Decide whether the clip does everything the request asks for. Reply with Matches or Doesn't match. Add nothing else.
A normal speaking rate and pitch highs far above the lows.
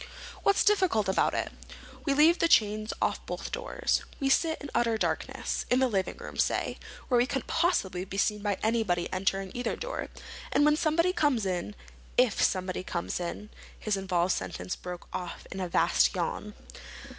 Matches